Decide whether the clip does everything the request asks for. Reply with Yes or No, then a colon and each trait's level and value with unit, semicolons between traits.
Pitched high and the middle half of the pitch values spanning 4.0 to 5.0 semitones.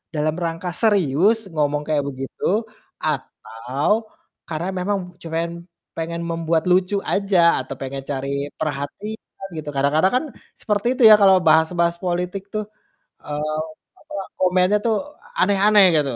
No: medium, 165 Hz; average, 4.7 semitones